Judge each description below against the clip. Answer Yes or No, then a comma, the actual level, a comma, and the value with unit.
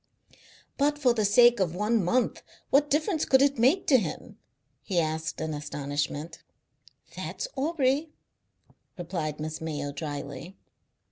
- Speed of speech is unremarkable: No, slow, 130 wpm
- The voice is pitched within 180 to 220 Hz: Yes, high, 190 Hz